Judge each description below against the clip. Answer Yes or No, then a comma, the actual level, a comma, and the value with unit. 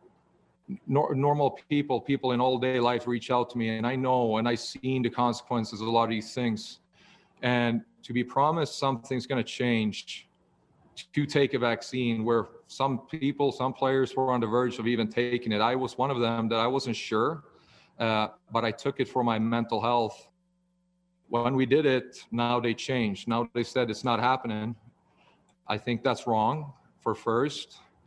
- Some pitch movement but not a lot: No, narrow, 2.2 semitones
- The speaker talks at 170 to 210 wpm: Yes, average, 185 wpm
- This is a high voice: No, low, 120 Hz